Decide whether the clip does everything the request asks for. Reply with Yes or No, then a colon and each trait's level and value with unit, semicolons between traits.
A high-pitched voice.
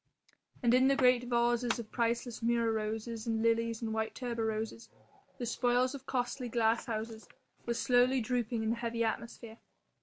Yes: high, 235 Hz